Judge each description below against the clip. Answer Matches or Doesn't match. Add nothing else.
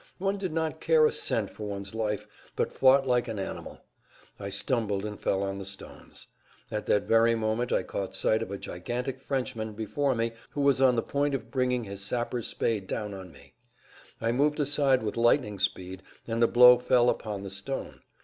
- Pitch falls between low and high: Doesn't match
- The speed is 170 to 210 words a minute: Matches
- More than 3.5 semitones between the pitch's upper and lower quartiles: Matches